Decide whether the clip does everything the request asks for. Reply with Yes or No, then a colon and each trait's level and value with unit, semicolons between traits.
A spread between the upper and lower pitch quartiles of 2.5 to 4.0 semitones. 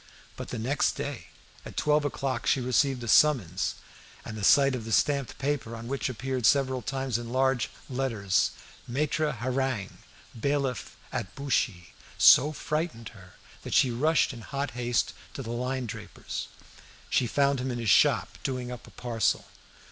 Yes: average, 3.0 semitones